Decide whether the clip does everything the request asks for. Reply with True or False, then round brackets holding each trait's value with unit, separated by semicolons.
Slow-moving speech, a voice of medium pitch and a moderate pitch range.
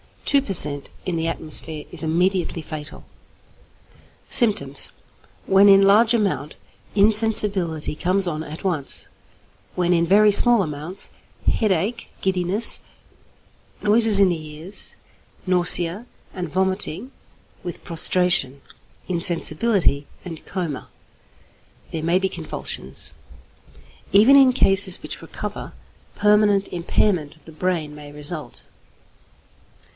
True (110 wpm; 180 Hz; 4.1 semitones)